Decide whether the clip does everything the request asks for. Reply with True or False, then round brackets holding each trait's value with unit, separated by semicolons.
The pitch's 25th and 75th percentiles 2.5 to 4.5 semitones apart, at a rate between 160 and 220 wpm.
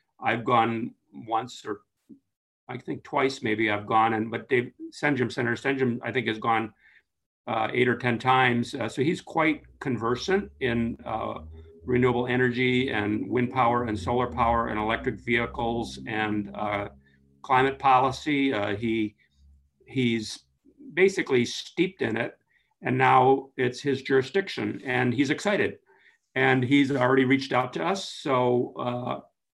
False (3.0 semitones; 140 wpm)